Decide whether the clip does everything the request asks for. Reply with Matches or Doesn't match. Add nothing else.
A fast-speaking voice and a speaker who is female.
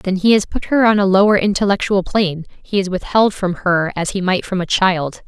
Matches